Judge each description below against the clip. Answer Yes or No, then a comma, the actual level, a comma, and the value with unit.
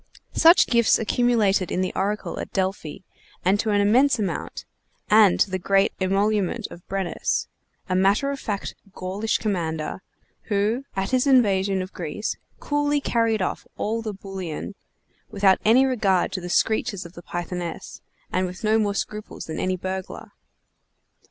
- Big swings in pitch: No, average, 3.0 semitones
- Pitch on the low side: No, high, 200 Hz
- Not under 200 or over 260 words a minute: No, average, 155 wpm